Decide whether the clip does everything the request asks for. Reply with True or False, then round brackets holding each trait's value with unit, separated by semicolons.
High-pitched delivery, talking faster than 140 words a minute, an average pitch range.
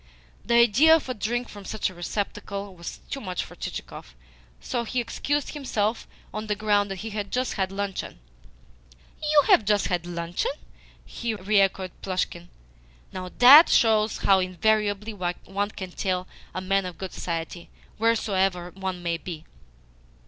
True (200 Hz; 155 wpm; 3.2 semitones)